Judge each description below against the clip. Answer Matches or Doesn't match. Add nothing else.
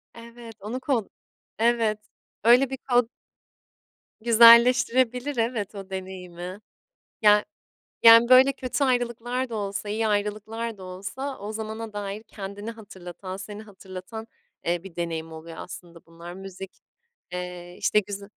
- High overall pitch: Matches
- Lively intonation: Doesn't match